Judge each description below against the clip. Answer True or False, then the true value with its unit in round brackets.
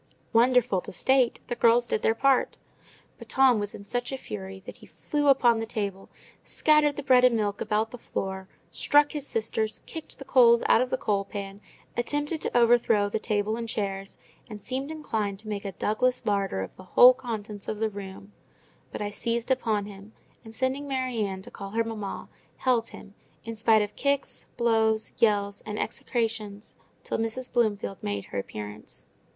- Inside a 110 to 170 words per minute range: False (185 wpm)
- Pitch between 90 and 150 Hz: False (225 Hz)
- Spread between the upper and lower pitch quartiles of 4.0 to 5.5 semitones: False (3.6 semitones)